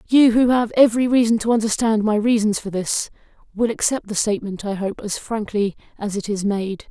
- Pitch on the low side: No, high, 215 Hz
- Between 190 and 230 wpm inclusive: Yes, average, 200 wpm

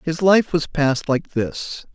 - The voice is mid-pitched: Yes, medium, 160 Hz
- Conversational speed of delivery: Yes, average, 185 wpm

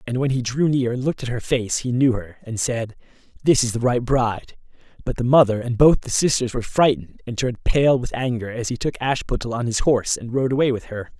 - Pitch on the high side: No, low, 125 Hz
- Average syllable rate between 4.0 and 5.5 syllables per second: No, 5.9 syllables/s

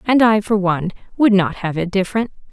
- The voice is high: Yes, high, 200 Hz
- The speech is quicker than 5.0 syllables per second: Yes, 6.1 syllables/s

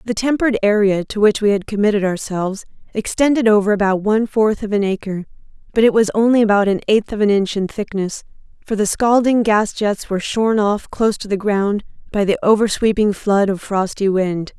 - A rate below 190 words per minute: No, average, 195 wpm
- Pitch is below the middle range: No, high, 210 Hz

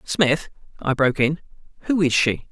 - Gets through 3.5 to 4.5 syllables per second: No, 4.8 syllables/s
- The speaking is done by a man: Yes, male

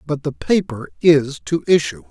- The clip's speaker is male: Yes, male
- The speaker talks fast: No, average, 170 wpm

